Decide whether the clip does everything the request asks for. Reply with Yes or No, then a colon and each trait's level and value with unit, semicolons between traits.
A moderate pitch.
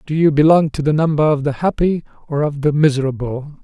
Yes: medium, 150 Hz